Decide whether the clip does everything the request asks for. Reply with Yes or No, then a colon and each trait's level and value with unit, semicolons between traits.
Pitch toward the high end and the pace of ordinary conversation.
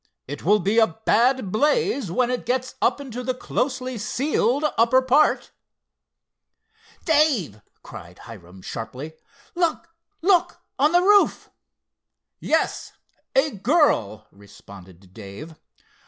No: high, 245 Hz; slow, 105 wpm